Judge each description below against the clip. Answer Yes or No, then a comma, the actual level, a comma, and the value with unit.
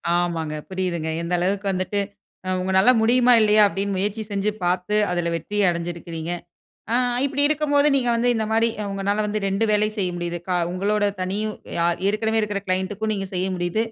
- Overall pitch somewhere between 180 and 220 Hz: Yes, high, 200 Hz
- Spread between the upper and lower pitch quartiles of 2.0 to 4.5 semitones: Yes, average, 3.1 semitones